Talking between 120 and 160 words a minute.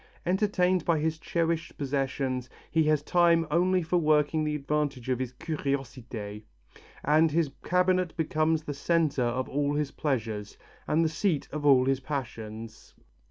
Yes: average, 155 wpm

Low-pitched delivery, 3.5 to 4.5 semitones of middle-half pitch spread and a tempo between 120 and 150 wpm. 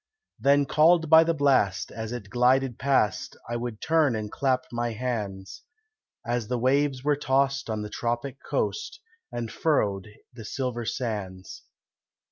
Yes: low, 125 Hz; average, 4.1 semitones; average, 145 wpm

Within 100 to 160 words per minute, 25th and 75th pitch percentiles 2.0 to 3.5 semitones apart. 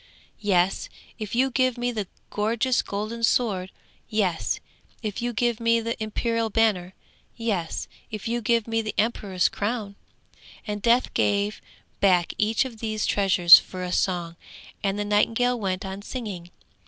Yes: average, 150 wpm; average, 3.0 semitones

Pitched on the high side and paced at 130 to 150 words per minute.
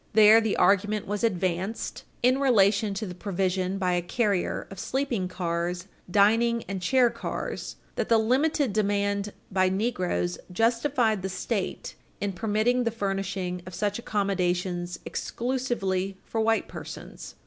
Yes: high, 200 Hz; slow, 135 wpm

